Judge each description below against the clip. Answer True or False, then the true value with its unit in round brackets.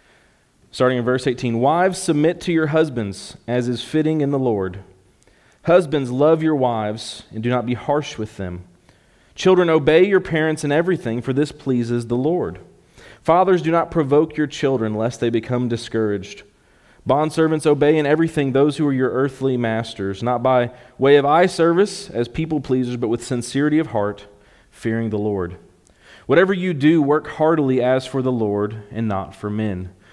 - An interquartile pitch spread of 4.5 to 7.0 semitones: True (5.6 semitones)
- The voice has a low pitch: True (130 Hz)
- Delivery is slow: False (175 wpm)